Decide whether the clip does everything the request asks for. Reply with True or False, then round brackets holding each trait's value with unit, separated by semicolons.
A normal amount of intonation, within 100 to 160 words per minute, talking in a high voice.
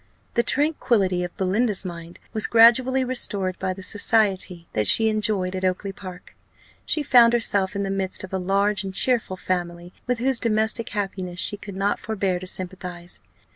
False (3.4 semitones; 175 wpm; 195 Hz)